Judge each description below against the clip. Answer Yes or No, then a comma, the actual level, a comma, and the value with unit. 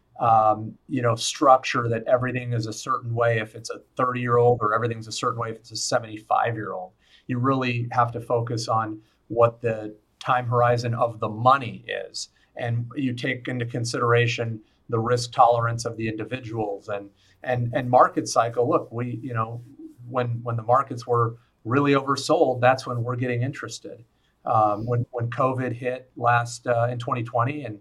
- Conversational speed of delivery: Yes, average, 180 wpm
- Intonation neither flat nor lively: No, narrow, 1.6 semitones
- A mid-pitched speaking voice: No, low, 120 Hz